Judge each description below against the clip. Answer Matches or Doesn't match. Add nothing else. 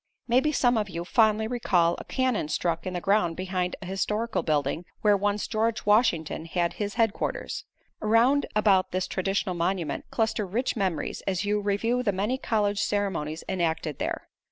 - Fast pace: Doesn't match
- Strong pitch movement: Doesn't match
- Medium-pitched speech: Doesn't match